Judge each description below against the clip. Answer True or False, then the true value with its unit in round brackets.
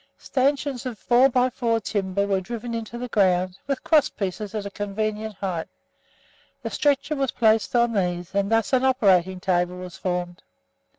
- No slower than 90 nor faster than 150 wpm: False (170 wpm)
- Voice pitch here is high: True (215 Hz)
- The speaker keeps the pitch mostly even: False (4.6 semitones)